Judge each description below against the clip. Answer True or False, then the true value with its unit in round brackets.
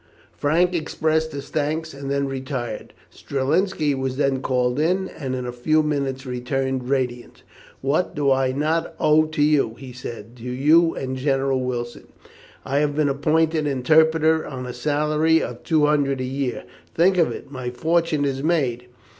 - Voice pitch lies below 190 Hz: True (140 Hz)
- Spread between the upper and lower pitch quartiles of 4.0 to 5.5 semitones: False (3.3 semitones)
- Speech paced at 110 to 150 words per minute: False (165 wpm)